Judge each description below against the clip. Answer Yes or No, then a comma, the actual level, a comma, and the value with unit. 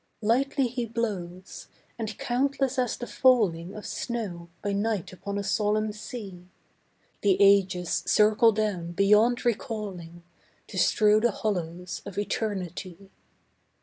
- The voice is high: Yes, high, 210 Hz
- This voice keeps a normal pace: No, slow, 120 wpm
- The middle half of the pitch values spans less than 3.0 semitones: No, average, 3.6 semitones